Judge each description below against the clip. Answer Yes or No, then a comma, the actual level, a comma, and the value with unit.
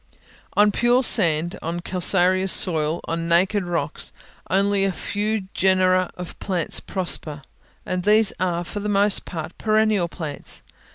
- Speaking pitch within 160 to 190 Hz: Yes, medium, 185 Hz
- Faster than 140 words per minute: No, slow, 135 wpm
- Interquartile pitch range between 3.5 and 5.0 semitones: No, average, 3.0 semitones